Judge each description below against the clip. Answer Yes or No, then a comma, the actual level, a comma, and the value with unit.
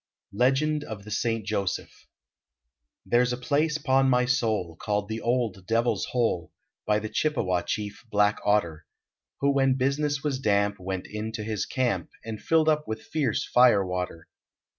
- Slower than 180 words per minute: Yes, average, 160 wpm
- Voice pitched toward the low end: Yes, low, 115 Hz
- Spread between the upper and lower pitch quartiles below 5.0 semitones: Yes, average, 4.5 semitones